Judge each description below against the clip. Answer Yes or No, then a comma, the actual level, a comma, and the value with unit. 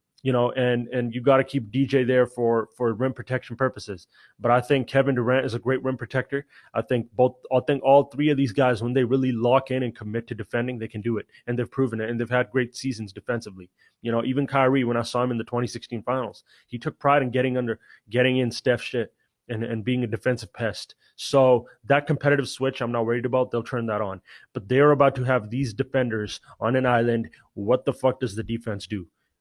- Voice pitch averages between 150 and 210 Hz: No, low, 125 Hz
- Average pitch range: No, narrow, 2.1 semitones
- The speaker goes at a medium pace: No, fast, 235 wpm